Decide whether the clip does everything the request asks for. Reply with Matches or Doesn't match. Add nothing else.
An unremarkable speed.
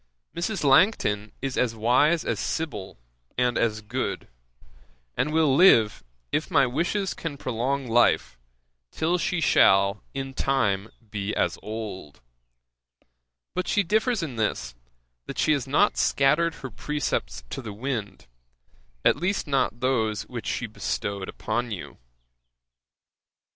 Doesn't match